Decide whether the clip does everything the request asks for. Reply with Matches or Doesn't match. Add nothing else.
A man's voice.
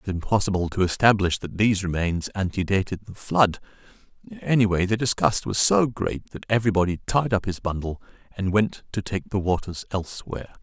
Matches